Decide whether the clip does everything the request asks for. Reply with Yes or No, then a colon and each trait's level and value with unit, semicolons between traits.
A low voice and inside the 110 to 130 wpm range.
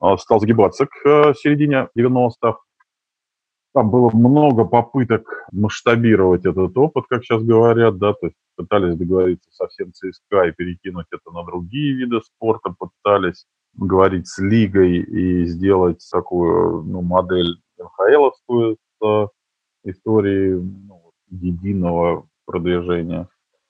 Yes: low, 100 Hz; average, 115 wpm